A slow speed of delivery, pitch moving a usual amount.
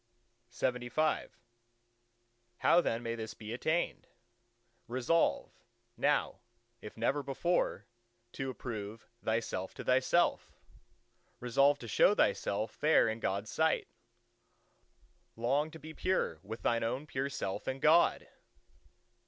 Yes: slow, 110 wpm; average, 4.3 semitones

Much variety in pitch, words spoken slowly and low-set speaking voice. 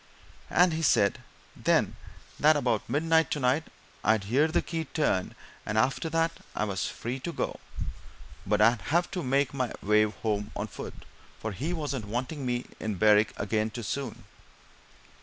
No: wide, 6.4 semitones; average, 170 wpm; low, 125 Hz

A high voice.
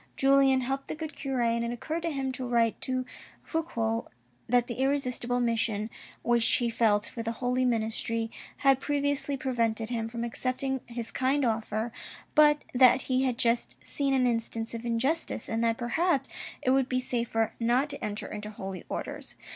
Yes: high, 245 Hz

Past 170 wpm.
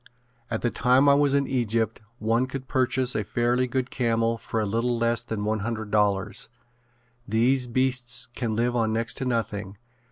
Yes: average, 180 wpm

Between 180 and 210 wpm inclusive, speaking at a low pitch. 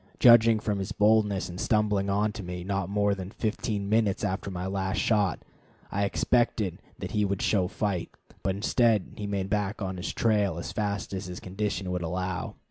Yes: average, 190 wpm; low, 100 Hz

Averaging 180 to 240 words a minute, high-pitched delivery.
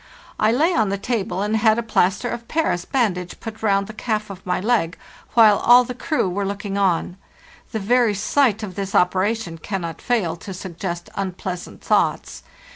Yes: average, 185 wpm; high, 200 Hz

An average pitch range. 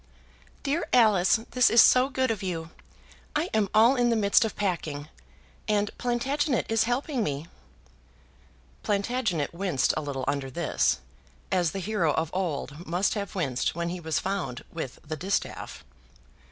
No: wide, 6.2 semitones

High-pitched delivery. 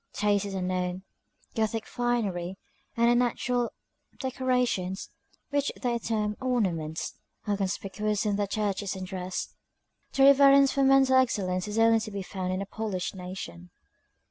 Yes: high, 210 Hz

